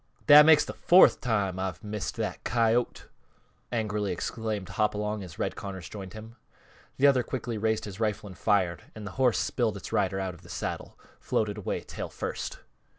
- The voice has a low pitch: Yes, low, 105 Hz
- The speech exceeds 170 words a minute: Yes, average, 180 wpm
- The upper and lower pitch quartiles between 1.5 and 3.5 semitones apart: Yes, average, 2.9 semitones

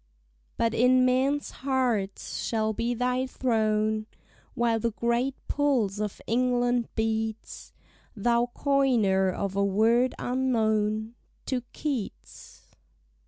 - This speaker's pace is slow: Yes, slow, 105 wpm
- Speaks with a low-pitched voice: No, high, 235 Hz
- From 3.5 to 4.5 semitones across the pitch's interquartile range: No, average, 2.7 semitones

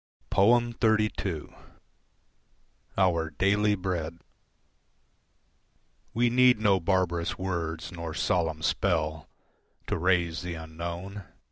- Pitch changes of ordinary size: Yes, average, 3.6 semitones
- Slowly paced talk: Yes, slow, 85 wpm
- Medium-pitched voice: No, very low, 90 Hz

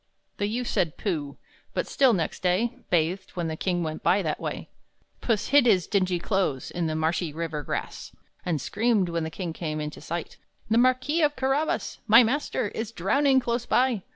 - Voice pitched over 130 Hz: Yes, high, 190 Hz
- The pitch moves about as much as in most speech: No, wide, 6.6 semitones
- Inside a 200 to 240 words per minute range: No, average, 185 wpm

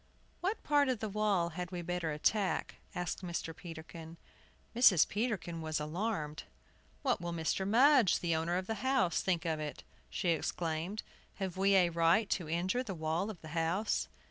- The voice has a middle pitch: Yes, medium, 175 Hz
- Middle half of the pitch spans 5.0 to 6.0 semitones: No, average, 4.3 semitones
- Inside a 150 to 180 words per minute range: Yes, average, 170 wpm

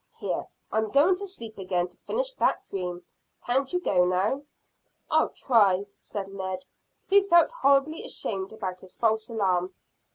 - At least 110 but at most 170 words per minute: Yes, average, 155 wpm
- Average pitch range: No, wide, 7.0 semitones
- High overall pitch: Yes, high, 215 Hz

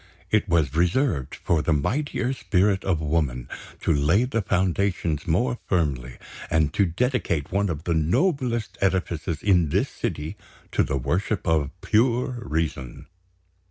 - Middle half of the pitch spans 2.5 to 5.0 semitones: No, wide, 5.5 semitones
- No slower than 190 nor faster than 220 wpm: No, average, 140 wpm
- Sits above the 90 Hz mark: No, very low, 85 Hz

